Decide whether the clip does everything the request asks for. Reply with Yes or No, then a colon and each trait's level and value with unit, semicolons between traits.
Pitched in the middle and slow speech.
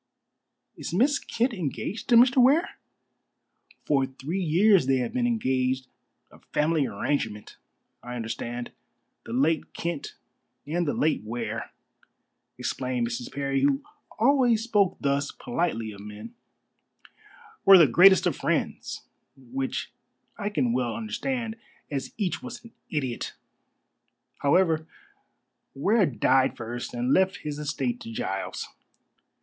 Yes: medium, 150 Hz; slow, 125 wpm